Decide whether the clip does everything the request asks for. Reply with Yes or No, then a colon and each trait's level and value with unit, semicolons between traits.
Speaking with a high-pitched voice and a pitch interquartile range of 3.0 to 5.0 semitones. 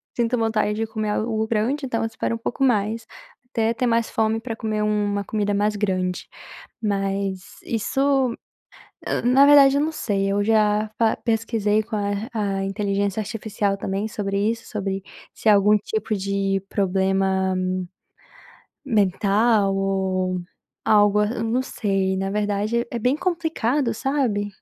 No: high, 210 Hz; narrow, 2.4 semitones